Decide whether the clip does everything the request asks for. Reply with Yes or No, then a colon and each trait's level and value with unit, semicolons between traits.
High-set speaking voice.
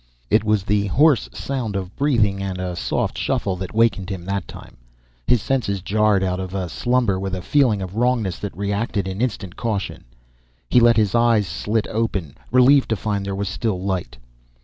No: low, 100 Hz